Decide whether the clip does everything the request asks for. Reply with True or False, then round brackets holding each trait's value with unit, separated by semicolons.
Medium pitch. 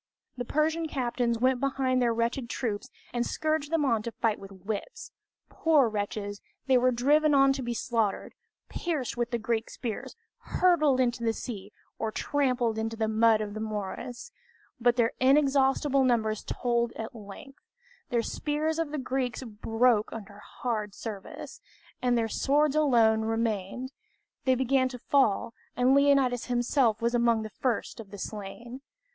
False (240 Hz)